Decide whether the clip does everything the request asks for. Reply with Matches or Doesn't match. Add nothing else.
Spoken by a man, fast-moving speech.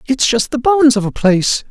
Matches